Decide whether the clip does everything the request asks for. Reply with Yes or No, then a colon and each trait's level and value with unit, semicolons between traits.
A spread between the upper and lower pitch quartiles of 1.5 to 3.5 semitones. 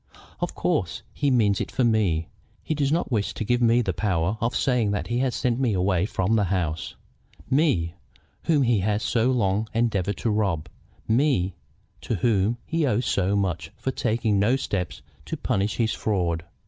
No: average, 4.3 semitones